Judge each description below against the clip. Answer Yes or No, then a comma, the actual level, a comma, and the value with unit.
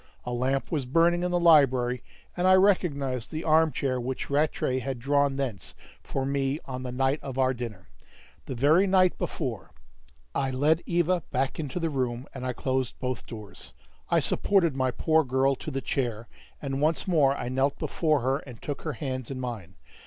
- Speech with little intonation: No, average, 3.5 semitones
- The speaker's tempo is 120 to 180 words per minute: No, average, 190 wpm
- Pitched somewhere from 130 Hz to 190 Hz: Yes, low, 135 Hz